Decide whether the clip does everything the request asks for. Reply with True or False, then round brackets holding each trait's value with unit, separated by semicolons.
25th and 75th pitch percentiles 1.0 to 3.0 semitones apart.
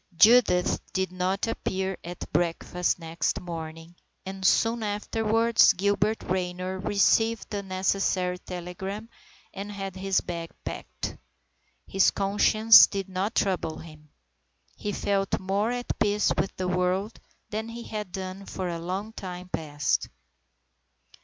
True (2.5 semitones)